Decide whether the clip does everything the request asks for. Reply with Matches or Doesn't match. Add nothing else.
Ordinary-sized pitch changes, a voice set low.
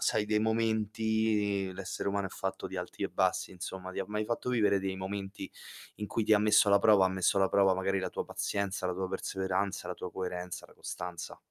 Doesn't match